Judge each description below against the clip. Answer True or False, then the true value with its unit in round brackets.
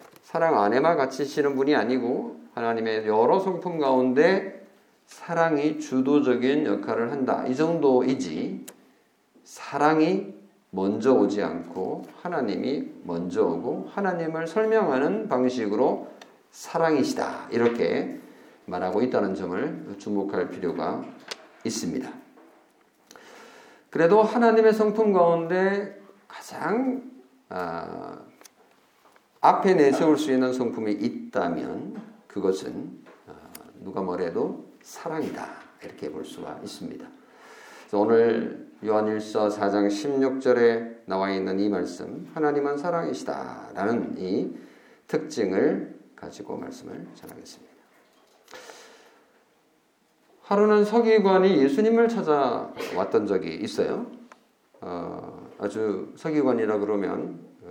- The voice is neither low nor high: True (145 Hz)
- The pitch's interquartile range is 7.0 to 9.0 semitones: True (8.5 semitones)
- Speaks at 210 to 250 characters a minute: True (235 characters per minute)